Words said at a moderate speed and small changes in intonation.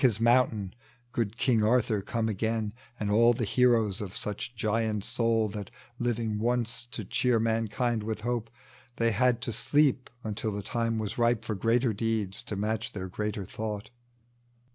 Yes: average, 165 wpm; narrow, 2.1 semitones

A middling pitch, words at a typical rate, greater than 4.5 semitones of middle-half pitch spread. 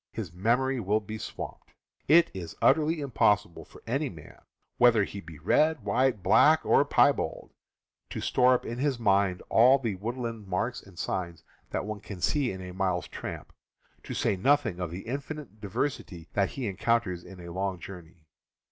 No: low, 105 Hz; average, 180 wpm; wide, 5.6 semitones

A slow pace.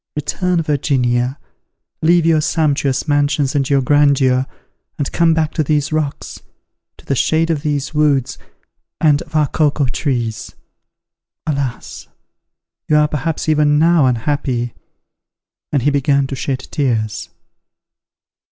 Yes: slow, 125 wpm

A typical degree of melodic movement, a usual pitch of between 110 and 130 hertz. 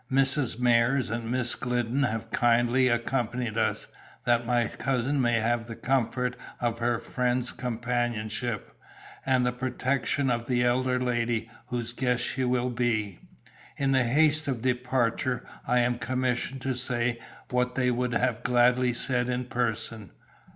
No: narrow, 1.2 semitones; low, 125 Hz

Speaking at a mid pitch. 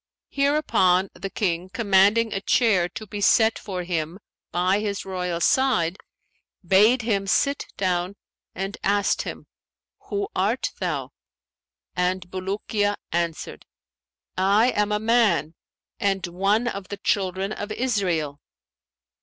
No: high, 195 Hz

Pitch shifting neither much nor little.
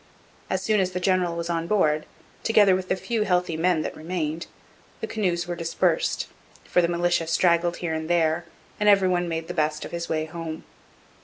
No: narrow, 2.1 semitones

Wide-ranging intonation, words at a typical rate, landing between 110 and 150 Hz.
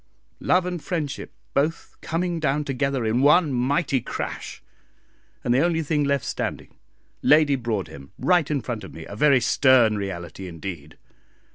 Yes: wide, 5.9 semitones; average, 150 wpm; low, 135 Hz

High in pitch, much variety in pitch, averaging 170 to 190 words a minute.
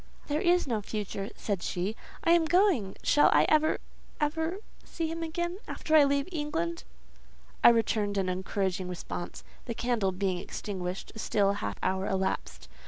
No: high, 215 Hz; wide, 8.7 semitones; average, 150 wpm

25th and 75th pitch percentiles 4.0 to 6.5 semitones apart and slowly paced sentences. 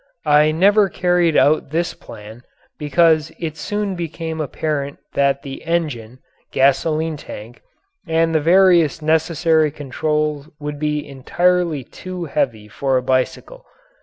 No: average, 3.0 semitones; slow, 125 wpm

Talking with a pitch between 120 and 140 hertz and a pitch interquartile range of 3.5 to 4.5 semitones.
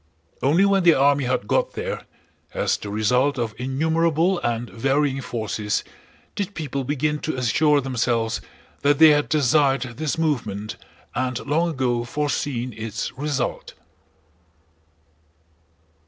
Yes: low, 135 Hz; average, 4.0 semitones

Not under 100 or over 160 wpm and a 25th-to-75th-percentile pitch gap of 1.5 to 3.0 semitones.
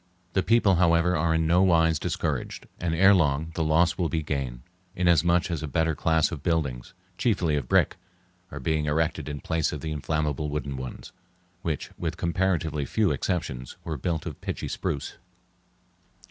No: average, 170 wpm; narrow, 2.6 semitones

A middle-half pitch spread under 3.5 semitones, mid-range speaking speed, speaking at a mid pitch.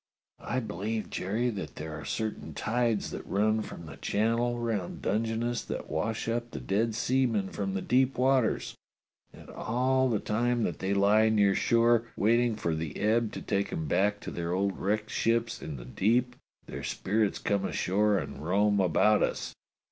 No: average, 3.1 semitones; average, 175 wpm; low, 110 Hz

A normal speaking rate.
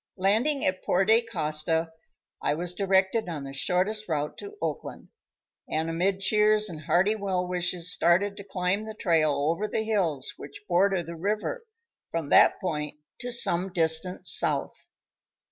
Yes: average, 150 wpm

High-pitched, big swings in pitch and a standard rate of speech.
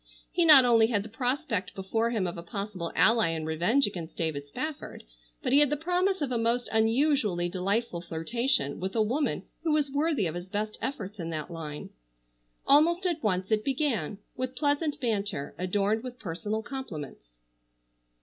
Yes: high, 220 Hz; wide, 7.3 semitones; average, 175 wpm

